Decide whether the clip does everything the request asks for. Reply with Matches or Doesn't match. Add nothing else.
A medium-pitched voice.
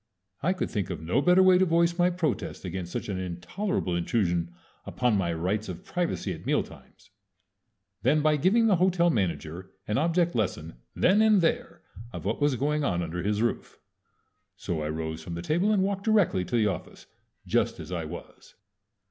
Doesn't match